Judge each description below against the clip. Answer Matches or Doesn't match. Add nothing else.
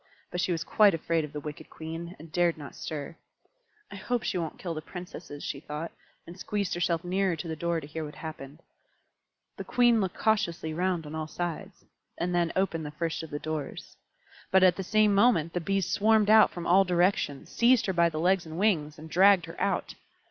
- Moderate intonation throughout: Matches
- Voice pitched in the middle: Matches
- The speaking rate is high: Matches